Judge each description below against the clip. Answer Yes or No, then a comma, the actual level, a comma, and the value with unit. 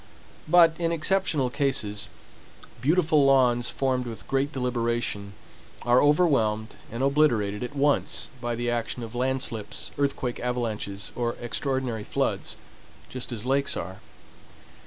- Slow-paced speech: Yes, slow, 125 wpm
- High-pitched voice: No, low, 125 Hz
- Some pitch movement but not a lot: Yes, average, 3.3 semitones